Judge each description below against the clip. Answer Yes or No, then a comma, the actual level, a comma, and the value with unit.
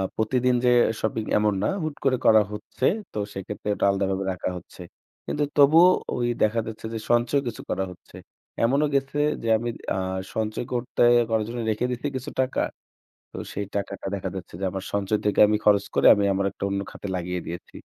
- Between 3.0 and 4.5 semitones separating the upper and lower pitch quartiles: Yes, average, 3.9 semitones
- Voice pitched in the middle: No, low, 110 Hz